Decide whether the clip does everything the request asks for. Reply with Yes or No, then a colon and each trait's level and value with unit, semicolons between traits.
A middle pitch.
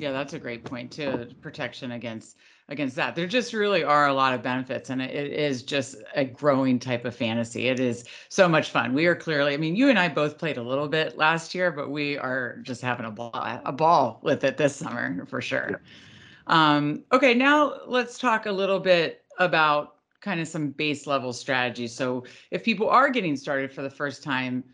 Yes: medium, 145 Hz